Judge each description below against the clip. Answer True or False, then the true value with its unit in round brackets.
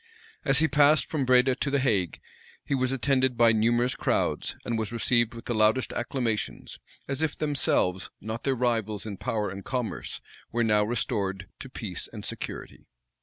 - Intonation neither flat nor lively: True (3.5 semitones)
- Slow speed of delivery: False (170 wpm)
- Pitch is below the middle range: True (120 Hz)